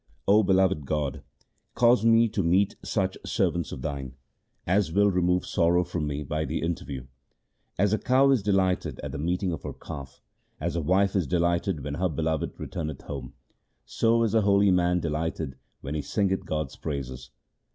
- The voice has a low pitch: Yes, very low, 85 Hz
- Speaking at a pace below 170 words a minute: No, average, 175 wpm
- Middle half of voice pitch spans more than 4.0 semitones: Yes, average, 4.6 semitones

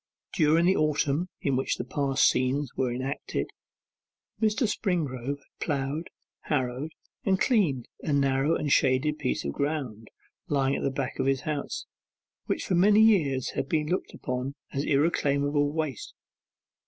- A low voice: No, medium, 145 Hz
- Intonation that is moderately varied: Yes, average, 3.0 semitones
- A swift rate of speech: No, average, 150 wpm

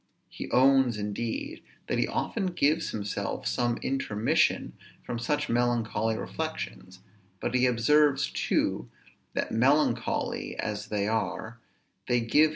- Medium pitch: No, low, 120 Hz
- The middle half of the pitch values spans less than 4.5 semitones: Yes, average, 3.6 semitones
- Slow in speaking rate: Yes, slow, 130 wpm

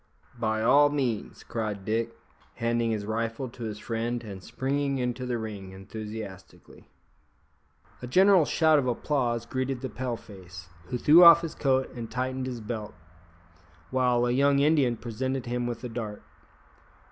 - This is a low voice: Yes, low, 120 Hz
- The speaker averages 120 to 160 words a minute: Yes, average, 155 wpm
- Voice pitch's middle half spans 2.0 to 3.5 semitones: Yes, average, 3.0 semitones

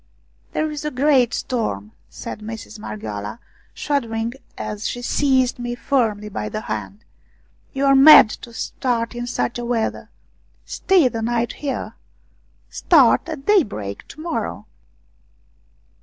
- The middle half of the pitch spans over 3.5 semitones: Yes, average, 4.5 semitones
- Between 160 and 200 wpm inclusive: No, average, 140 wpm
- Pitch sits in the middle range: No, high, 240 Hz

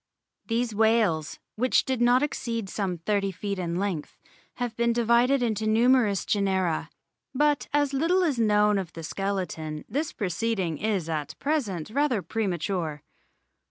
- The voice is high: Yes, high, 215 Hz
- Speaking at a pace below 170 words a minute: Yes, average, 140 wpm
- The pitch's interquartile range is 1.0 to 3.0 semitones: No, average, 4.8 semitones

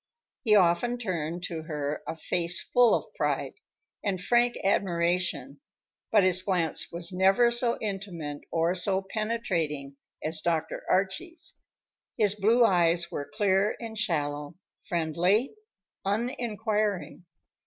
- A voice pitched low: No, medium, 185 Hz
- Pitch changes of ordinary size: Yes, average, 4.3 semitones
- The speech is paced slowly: Yes, slow, 120 wpm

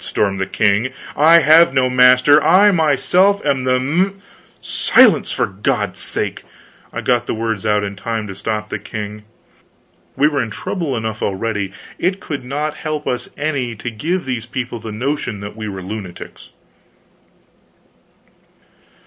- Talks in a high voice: No, low, 125 Hz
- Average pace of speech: Yes, average, 155 wpm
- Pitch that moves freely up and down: Yes, wide, 5.8 semitones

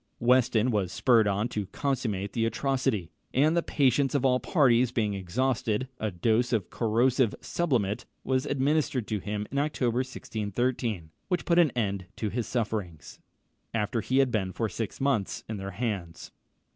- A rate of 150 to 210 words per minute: Yes, average, 160 wpm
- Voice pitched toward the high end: No, low, 115 Hz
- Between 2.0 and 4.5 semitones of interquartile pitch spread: Yes, average, 4.0 semitones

